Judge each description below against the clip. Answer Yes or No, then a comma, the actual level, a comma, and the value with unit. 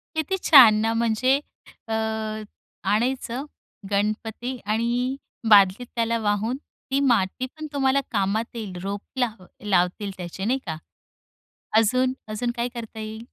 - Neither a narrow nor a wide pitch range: Yes, average, 3.4 semitones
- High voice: Yes, high, 225 Hz